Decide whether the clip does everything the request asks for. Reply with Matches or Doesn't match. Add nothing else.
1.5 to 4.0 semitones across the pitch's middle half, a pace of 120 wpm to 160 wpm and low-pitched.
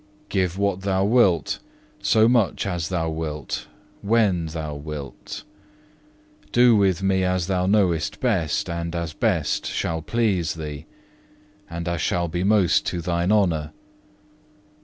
Matches